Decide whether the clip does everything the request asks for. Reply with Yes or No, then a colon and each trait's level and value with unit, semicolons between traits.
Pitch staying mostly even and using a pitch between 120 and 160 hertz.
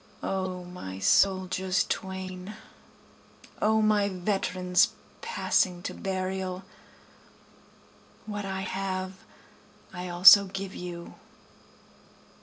No: narrow, 1.2 semitones; medium, 185 Hz